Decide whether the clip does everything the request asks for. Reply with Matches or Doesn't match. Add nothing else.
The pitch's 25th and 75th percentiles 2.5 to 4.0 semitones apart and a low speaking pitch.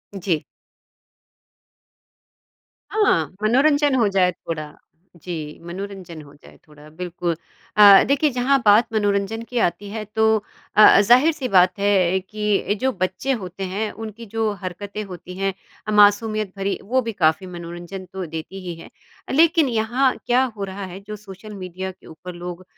Doesn't match